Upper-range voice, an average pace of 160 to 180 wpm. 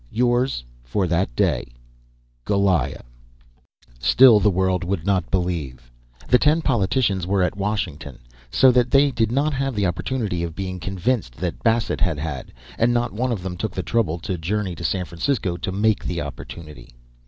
No: very low, 95 Hz; average, 175 wpm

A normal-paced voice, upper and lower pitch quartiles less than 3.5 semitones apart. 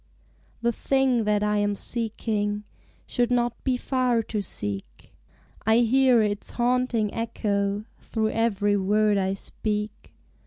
No: slow, 130 wpm; narrow, 2.6 semitones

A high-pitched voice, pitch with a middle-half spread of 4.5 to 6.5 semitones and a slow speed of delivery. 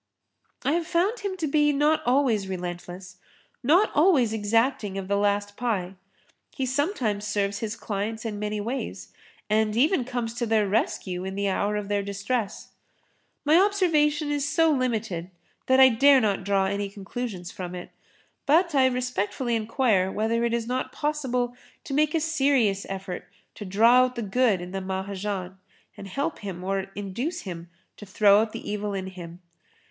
No: high, 220 Hz; average, 5.2 semitones; average, 175 wpm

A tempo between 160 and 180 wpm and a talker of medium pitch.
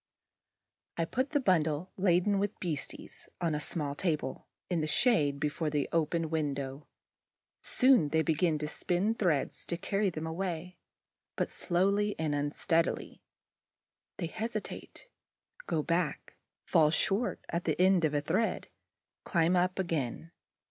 No: slow, 135 wpm; medium, 165 Hz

